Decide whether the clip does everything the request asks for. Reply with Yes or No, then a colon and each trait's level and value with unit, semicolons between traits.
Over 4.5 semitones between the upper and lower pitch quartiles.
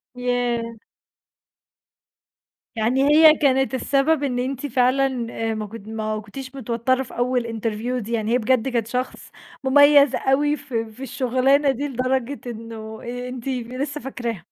No: average, 2.8 semitones